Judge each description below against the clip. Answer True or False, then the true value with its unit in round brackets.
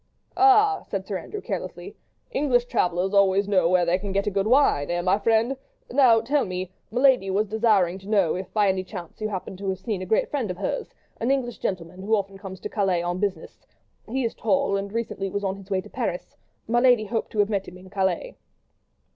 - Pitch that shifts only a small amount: False (3.6 semitones)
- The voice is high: True (200 Hz)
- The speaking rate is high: True (215 wpm)